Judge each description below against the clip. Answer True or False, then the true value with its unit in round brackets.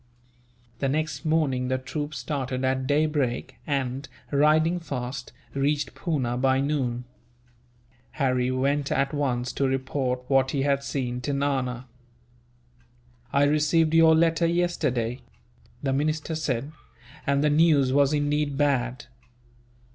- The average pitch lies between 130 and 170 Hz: True (140 Hz)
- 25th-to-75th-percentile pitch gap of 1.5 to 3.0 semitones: True (2.7 semitones)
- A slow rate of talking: True (125 wpm)